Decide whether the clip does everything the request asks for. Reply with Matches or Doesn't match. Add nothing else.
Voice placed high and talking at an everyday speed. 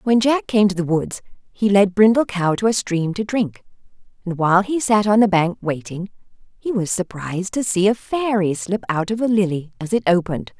Doesn't match